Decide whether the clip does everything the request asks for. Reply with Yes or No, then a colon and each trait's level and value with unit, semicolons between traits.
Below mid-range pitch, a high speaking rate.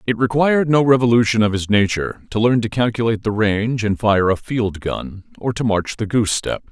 Yes: low, 110 Hz; fast, 215 wpm